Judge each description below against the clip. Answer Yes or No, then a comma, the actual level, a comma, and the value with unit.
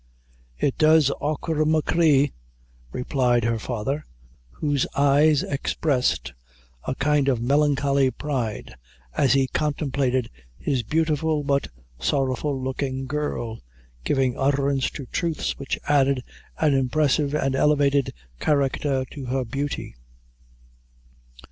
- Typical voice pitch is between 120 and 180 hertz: Yes, medium, 140 Hz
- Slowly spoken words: Yes, slow, 105 wpm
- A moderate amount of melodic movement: No, narrow, 2.2 semitones